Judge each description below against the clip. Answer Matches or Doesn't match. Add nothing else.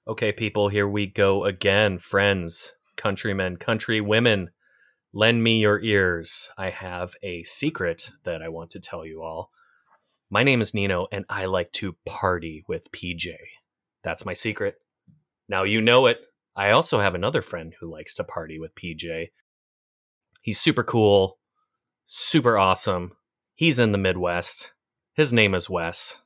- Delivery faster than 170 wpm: Doesn't match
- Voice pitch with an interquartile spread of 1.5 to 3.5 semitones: Doesn't match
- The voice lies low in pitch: Matches